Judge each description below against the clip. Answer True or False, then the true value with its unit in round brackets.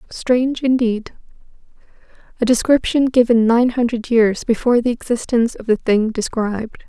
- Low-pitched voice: False (235 Hz)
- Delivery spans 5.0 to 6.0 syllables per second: True (5.1 syllables/s)